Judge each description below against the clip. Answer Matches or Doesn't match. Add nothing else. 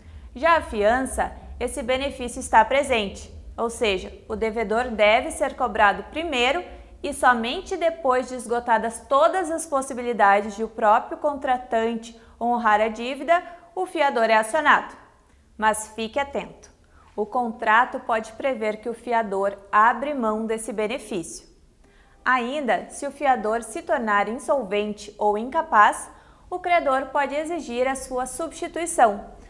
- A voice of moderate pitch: Doesn't match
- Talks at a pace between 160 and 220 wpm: Doesn't match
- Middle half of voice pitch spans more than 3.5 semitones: Matches